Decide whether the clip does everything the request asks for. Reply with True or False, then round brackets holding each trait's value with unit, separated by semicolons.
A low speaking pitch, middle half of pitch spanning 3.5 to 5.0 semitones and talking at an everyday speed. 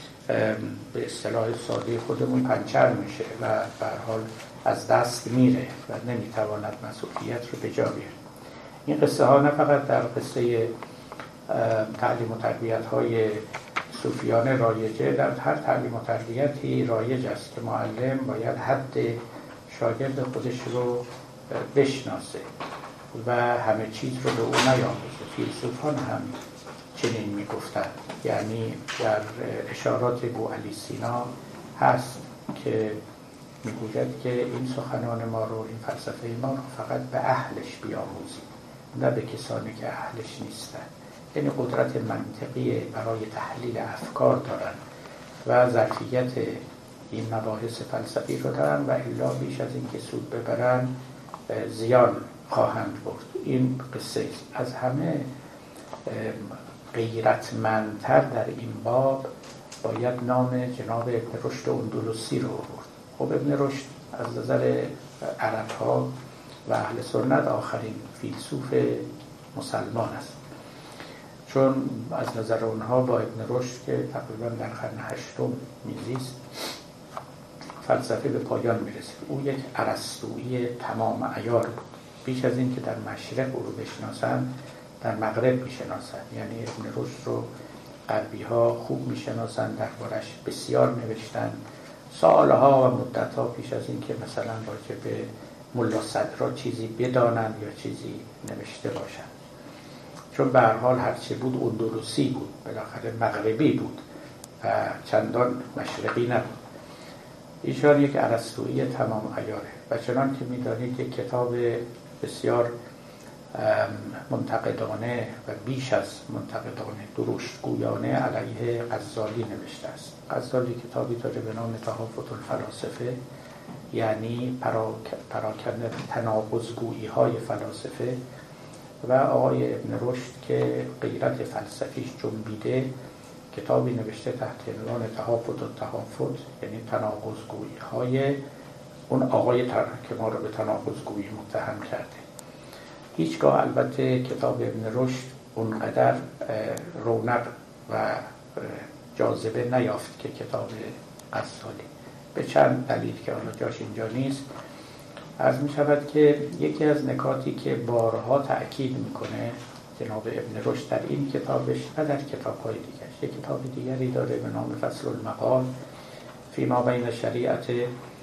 False (120 Hz; 2.5 semitones; 120 wpm)